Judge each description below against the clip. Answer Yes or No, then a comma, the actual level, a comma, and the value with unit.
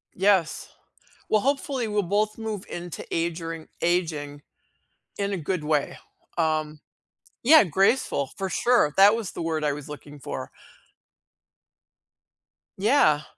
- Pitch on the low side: No, medium, 175 Hz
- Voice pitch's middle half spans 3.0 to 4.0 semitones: No, wide, 5.4 semitones